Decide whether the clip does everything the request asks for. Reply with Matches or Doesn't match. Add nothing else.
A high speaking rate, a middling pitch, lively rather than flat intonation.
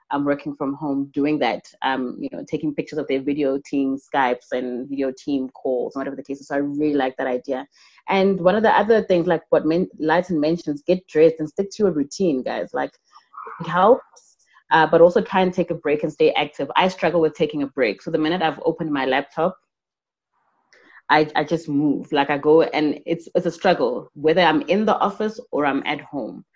Doesn't match